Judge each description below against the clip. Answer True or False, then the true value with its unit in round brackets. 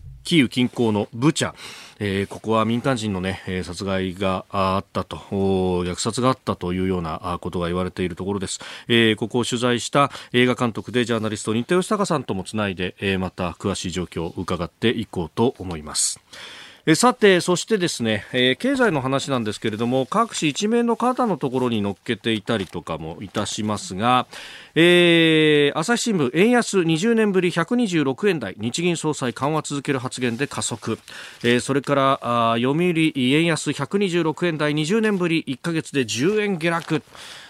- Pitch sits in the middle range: False (125 Hz)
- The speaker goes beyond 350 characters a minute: False (325 characters per minute)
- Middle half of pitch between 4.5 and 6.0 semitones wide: False (7.8 semitones)